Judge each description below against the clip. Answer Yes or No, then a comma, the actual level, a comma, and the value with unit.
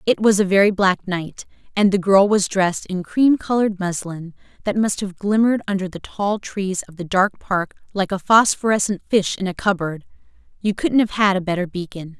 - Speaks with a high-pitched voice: Yes, high, 195 Hz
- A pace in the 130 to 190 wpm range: No, average, 200 wpm